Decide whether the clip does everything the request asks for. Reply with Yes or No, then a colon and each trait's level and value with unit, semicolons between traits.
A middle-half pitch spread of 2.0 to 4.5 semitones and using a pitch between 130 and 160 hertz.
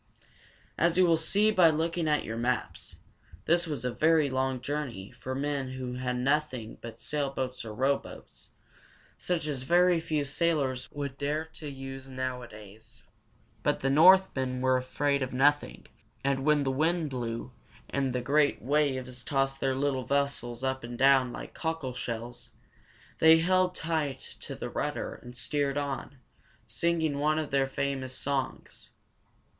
Yes: average, 3.0 semitones; medium, 140 Hz